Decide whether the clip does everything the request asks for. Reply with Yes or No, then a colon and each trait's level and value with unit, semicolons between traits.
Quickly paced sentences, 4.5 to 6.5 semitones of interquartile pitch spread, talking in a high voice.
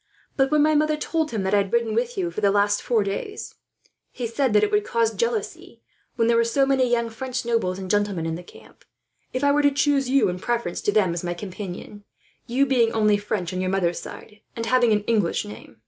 Yes: fast, 240 wpm; average, 5.0 semitones; high, 225 Hz